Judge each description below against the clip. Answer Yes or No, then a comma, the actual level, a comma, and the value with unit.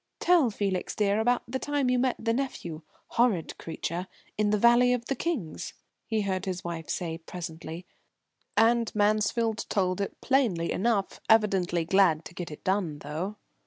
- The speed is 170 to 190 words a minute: No, average, 160 wpm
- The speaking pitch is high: Yes, high, 205 Hz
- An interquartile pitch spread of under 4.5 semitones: No, average, 5.2 semitones